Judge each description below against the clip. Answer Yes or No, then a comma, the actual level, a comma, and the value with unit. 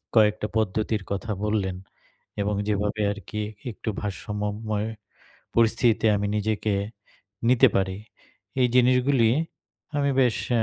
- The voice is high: No, low, 110 Hz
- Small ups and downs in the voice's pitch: Yes, narrow, 2.0 semitones